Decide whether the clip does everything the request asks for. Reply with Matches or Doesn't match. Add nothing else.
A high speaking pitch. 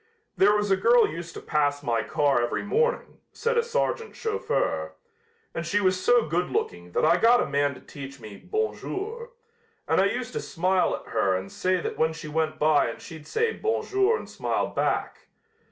Doesn't match